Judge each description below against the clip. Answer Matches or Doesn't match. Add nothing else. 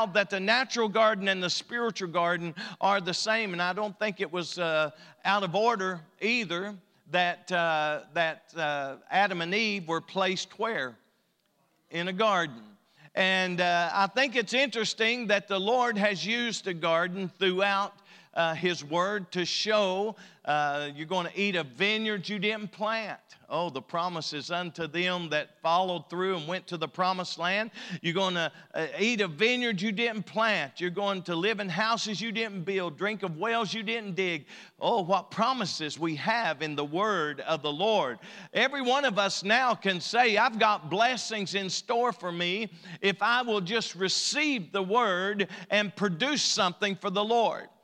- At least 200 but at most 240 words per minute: Doesn't match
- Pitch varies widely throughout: Doesn't match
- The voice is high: Matches